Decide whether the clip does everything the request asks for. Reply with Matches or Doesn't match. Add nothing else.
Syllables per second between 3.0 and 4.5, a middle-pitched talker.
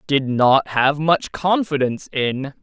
Matches